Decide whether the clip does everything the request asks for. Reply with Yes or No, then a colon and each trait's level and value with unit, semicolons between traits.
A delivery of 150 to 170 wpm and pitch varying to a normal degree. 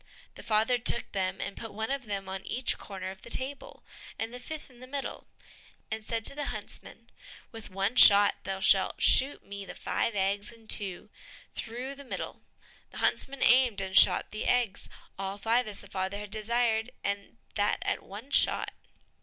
No: average, 185 wpm; average, 3.7 semitones